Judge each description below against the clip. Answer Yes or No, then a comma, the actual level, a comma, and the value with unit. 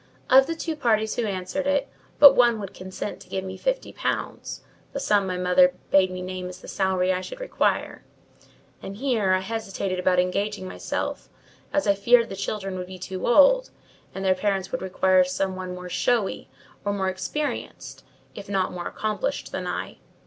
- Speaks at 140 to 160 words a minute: No, average, 185 wpm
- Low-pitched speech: No, high, 195 Hz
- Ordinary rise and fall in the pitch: Yes, average, 4.1 semitones